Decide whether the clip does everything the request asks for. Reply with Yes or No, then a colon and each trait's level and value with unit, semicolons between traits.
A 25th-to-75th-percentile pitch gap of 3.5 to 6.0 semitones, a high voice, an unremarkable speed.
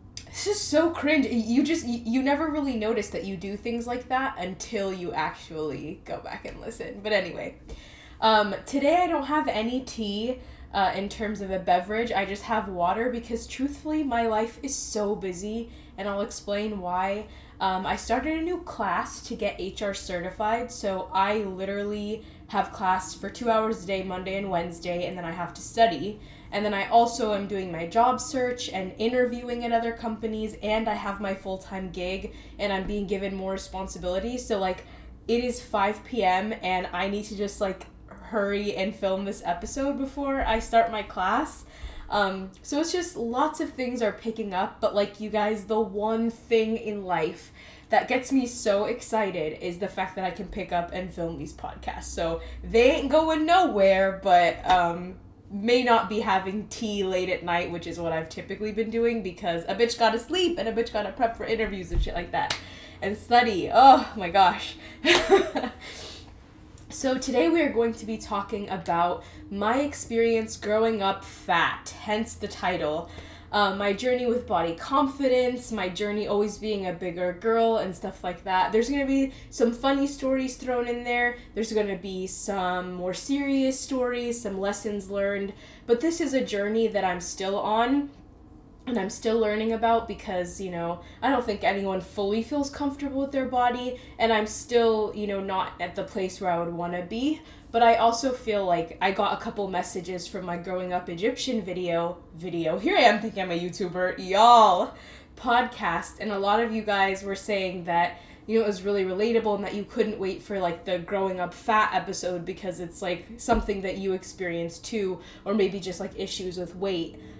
Yes: average, 3.8 semitones; high, 210 Hz; average, 190 wpm